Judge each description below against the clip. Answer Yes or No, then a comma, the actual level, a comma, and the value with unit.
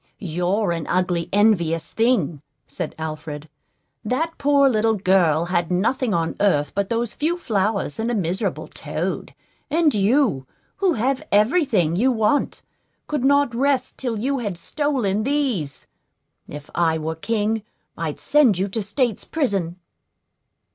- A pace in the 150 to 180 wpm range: No, average, 140 wpm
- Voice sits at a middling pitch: No, high, 210 Hz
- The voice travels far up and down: Yes, wide, 7.0 semitones